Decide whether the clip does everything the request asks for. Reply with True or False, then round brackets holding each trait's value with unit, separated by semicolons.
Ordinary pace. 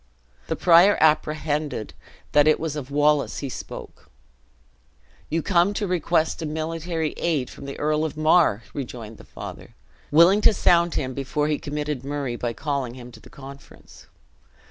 True (160 wpm)